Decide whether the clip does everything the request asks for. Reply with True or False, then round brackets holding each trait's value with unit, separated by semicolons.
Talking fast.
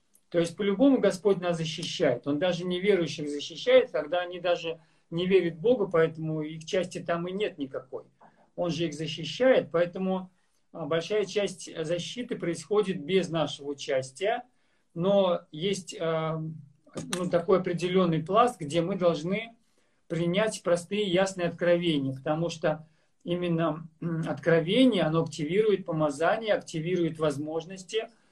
False (125 wpm)